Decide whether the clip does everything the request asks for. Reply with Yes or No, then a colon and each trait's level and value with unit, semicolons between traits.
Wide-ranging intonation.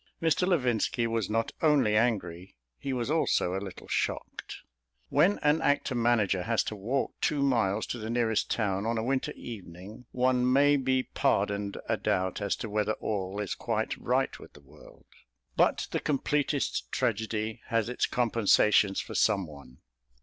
No: average, 4.2 semitones